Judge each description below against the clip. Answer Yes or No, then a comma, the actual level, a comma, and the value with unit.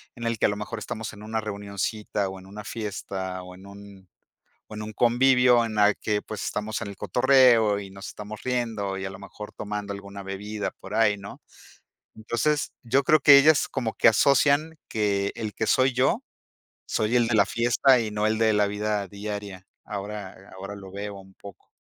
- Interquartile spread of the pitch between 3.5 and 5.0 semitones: No, narrow, 2.5 semitones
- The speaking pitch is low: Yes, low, 105 Hz